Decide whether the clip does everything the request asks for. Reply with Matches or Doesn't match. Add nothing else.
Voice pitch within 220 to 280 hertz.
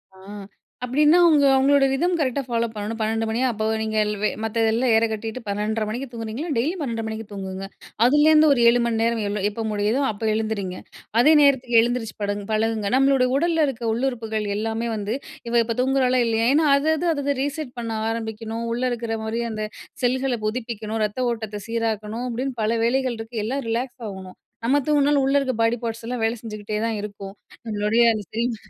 Matches